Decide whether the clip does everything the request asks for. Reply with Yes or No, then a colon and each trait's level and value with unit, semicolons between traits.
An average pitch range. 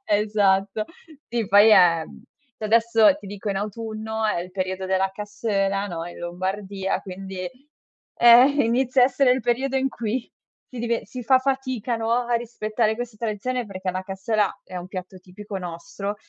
Yes: average, 3.6 semitones